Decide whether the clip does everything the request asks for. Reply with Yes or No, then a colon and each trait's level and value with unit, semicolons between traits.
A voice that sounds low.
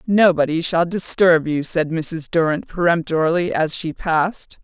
No: medium, 165 Hz